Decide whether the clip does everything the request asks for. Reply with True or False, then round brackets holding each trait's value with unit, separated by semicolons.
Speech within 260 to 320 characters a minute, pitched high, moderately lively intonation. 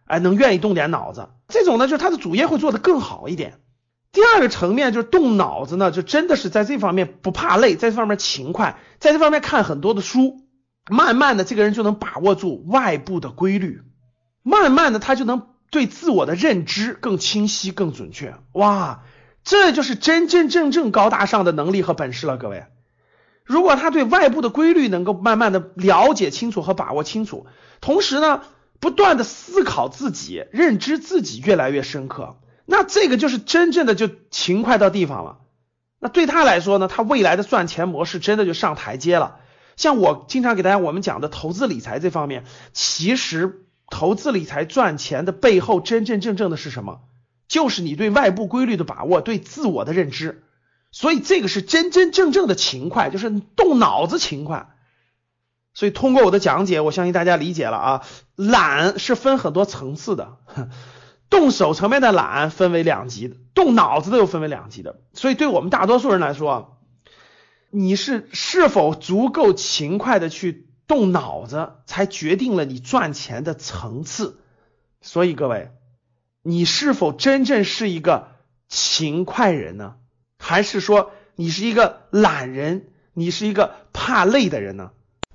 False (270 characters per minute; 195 Hz; 8.3 semitones)